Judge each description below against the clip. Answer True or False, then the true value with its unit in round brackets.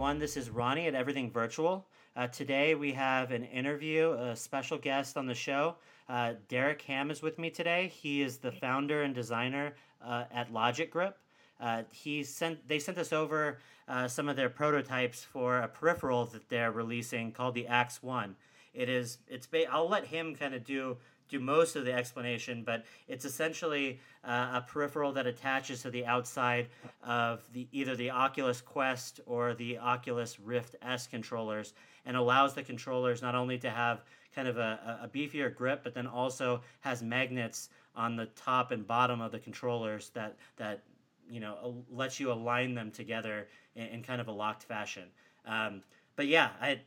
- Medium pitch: False (125 Hz)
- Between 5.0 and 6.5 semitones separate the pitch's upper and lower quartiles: False (2.8 semitones)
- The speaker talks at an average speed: True (185 wpm)